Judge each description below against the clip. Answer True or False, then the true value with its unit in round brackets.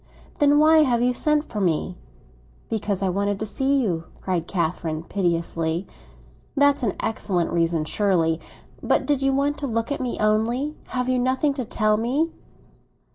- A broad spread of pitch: True (7.2 semitones)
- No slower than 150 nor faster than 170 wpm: True (165 wpm)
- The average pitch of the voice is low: False (220 Hz)